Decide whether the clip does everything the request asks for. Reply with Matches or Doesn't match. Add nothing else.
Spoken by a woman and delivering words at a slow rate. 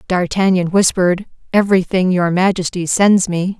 Matches